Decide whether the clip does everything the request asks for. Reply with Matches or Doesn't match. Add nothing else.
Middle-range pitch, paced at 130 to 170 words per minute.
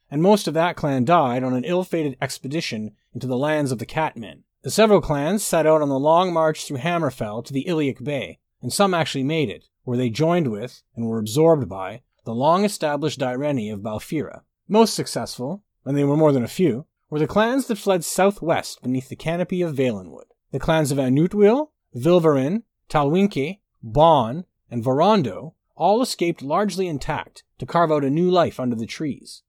Doesn't match